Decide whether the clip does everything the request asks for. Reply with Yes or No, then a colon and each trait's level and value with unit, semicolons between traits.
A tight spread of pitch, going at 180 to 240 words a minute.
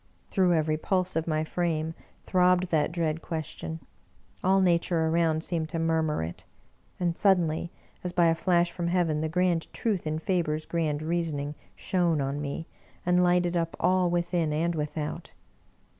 No: narrow, 2.1 semitones; average, 160 wpm